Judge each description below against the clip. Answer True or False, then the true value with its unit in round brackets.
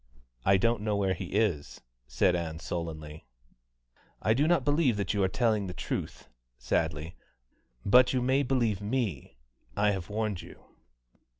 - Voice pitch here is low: True (100 Hz)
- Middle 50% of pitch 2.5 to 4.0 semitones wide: False (5.2 semitones)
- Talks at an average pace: True (145 wpm)